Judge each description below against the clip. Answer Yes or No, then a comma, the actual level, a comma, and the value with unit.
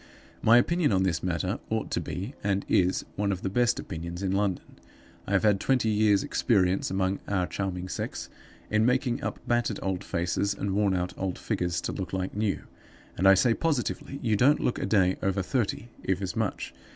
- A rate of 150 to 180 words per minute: No, average, 195 wpm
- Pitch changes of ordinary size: Yes, average, 3.0 semitones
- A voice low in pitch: Yes, low, 100 Hz